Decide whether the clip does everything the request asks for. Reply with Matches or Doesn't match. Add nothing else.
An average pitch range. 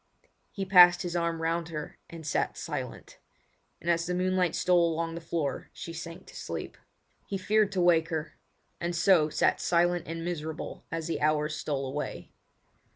Doesn't match